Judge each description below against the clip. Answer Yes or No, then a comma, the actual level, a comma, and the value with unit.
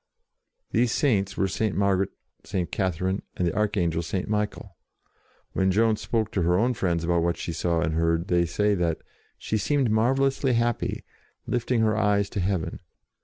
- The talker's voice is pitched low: Yes, low, 100 Hz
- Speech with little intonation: No, average, 4.1 semitones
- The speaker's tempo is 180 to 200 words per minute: No, average, 170 wpm